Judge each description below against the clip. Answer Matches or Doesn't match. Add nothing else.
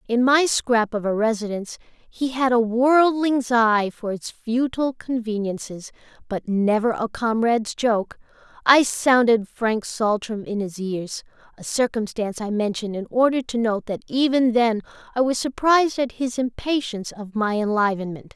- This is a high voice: Matches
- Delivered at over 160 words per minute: Doesn't match